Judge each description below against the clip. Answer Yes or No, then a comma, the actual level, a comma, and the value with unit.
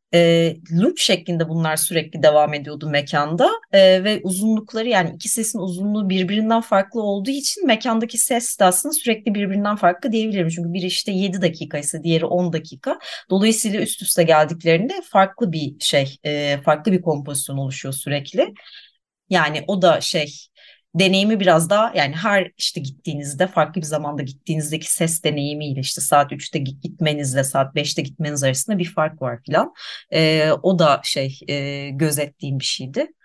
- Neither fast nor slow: No, fast, 150 wpm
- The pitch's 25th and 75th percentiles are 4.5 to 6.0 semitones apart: Yes, wide, 5.4 semitones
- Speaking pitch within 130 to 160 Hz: No, medium, 170 Hz